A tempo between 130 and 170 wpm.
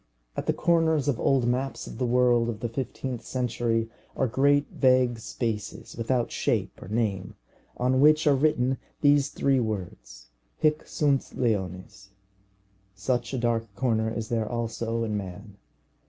Yes: average, 150 wpm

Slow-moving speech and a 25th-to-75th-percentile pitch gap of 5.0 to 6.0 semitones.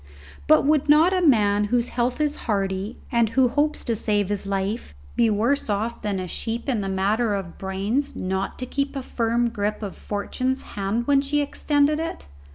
No: average, 190 wpm; average, 5.3 semitones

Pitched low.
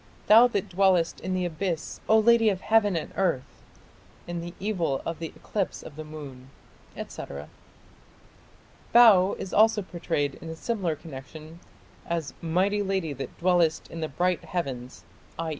No: medium, 175 Hz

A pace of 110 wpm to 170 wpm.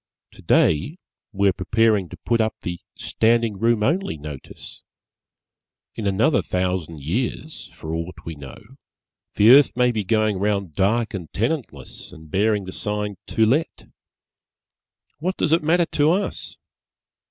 Yes: average, 140 wpm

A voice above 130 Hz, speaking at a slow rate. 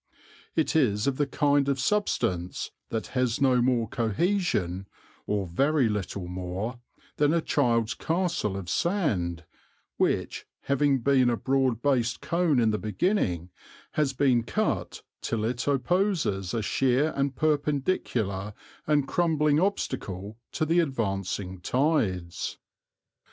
No: low, 125 Hz; slow, 125 wpm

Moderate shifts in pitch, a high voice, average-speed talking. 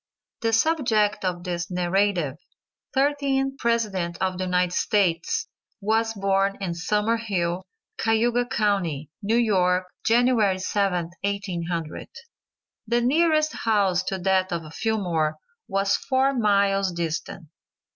No: average, 4.2 semitones; high, 195 Hz; slow, 115 wpm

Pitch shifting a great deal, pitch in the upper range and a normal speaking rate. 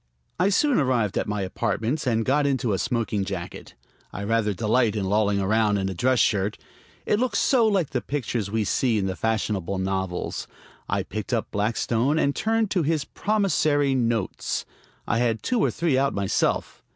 No: wide, 5.9 semitones; low, 115 Hz; average, 180 wpm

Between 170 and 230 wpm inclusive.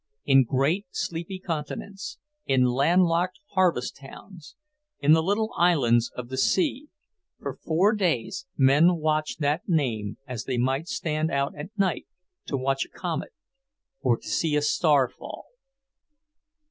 No: average, 145 wpm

